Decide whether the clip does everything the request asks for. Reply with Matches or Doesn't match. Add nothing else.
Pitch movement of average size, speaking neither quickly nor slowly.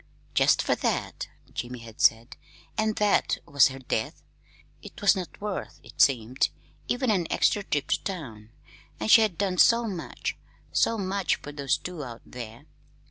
Doesn't match